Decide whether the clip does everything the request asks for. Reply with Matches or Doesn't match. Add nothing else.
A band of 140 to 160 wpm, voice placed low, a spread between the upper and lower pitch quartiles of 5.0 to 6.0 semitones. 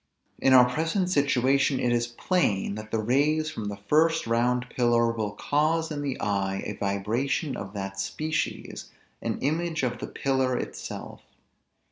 Matches